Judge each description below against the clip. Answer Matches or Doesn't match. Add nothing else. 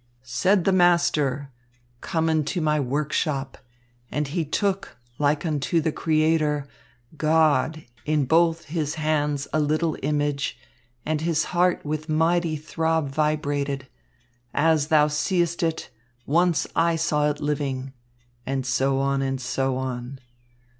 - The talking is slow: Matches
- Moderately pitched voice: Matches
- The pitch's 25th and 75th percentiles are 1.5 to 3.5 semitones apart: Matches